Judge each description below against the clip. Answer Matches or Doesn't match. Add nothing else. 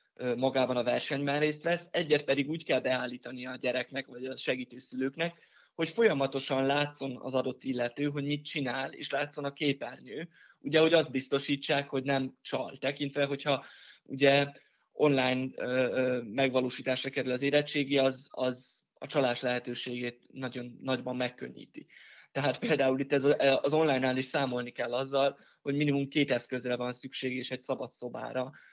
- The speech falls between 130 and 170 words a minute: Matches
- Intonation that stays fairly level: Matches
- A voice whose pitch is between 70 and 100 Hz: Doesn't match